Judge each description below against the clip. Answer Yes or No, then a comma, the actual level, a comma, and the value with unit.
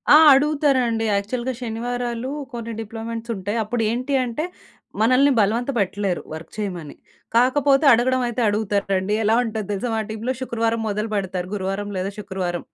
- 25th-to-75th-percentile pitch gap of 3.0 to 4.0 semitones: Yes, average, 3.4 semitones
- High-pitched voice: Yes, high, 225 Hz